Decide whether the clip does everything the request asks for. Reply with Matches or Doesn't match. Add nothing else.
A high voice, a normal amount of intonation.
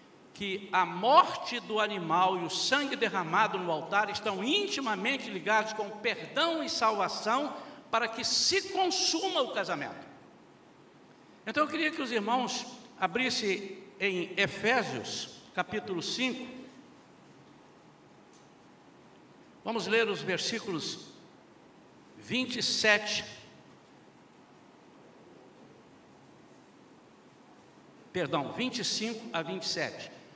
Matches